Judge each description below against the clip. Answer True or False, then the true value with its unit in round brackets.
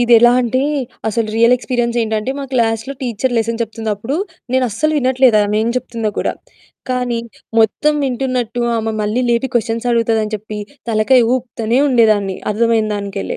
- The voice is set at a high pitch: True (230 Hz)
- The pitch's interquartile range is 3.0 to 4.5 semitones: False (2.4 semitones)